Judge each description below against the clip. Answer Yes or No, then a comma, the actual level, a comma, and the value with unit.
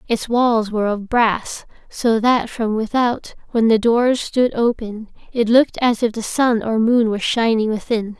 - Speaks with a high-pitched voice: Yes, high, 225 Hz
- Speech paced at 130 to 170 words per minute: No, average, 185 wpm